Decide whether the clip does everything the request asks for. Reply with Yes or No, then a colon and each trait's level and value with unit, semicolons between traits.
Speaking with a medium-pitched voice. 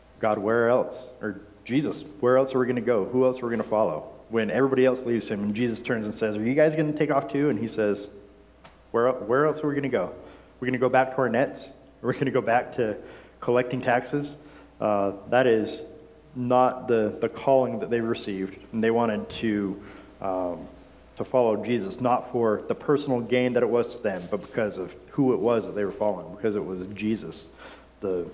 No: low, 120 Hz